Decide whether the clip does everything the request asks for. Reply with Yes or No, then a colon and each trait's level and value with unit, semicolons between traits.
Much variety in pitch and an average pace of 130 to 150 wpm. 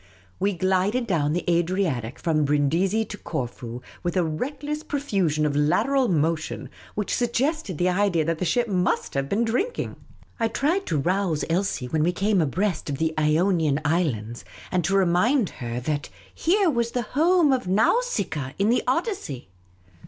No: wide, 7.2 semitones; average, 165 wpm